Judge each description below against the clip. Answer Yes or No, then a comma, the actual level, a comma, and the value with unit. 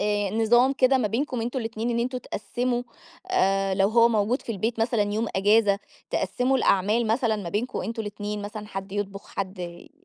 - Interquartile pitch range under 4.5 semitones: Yes, average, 3.0 semitones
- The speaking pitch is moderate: No, high, 220 Hz